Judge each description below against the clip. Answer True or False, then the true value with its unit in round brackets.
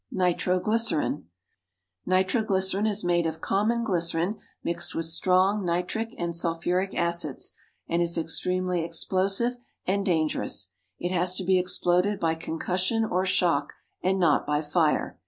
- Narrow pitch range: True (2.3 semitones)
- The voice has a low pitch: False (180 Hz)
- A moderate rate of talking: False (130 wpm)